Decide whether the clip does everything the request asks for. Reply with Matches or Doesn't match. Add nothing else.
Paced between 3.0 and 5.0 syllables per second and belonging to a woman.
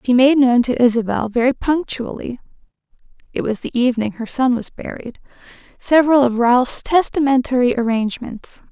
Doesn't match